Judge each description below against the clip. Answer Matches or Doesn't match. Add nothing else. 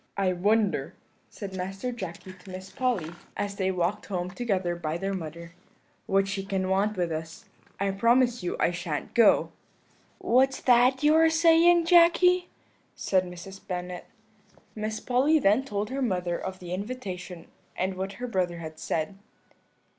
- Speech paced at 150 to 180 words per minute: Matches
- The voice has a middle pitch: Doesn't match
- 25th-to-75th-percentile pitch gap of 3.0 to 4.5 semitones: Doesn't match